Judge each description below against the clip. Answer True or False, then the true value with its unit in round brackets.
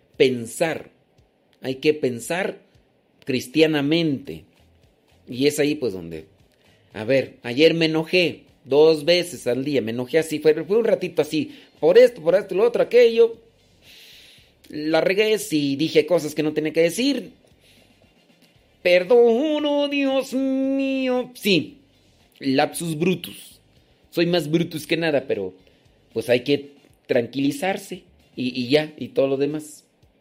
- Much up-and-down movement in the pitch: True (7.6 semitones)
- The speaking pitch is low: False (155 Hz)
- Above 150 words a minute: False (135 wpm)